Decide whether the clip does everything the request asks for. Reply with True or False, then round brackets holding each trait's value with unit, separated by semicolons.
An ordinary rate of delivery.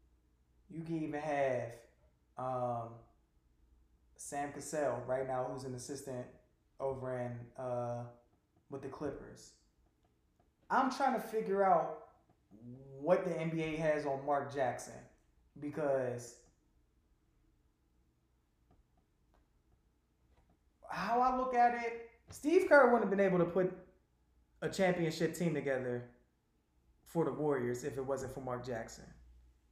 False (115 wpm)